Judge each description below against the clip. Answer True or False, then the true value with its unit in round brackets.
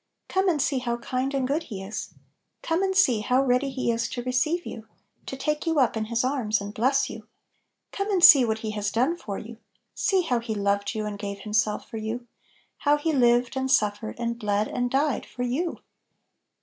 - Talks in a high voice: True (245 Hz)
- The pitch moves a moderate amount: True (4.4 semitones)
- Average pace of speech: False (215 wpm)